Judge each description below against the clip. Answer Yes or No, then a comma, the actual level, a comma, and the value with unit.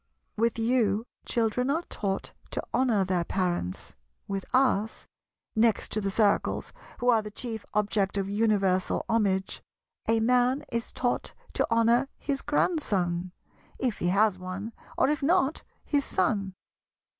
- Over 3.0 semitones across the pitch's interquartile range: Yes, average, 4.1 semitones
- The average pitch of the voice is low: No, high, 220 Hz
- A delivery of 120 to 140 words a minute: Yes, slow, 135 wpm